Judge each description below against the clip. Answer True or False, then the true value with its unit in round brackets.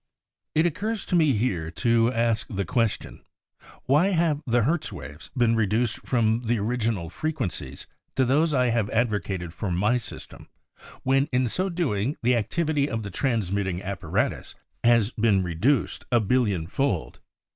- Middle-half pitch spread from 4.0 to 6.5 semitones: True (5.1 semitones)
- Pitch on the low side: True (115 Hz)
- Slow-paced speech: False (155 wpm)